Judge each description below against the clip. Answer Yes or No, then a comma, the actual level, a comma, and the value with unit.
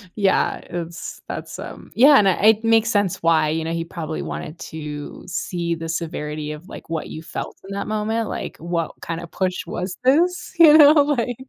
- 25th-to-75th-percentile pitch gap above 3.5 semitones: Yes, wide, 5.5 semitones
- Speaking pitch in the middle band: Yes, medium, 175 Hz